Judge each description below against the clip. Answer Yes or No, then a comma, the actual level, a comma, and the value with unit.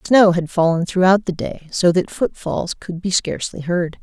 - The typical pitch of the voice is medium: Yes, medium, 180 Hz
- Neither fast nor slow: Yes, average, 195 wpm